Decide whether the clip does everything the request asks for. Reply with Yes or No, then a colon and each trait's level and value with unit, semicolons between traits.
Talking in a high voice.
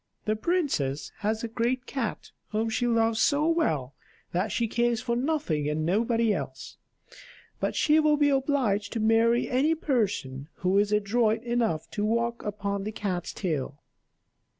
Yes: high, 225 Hz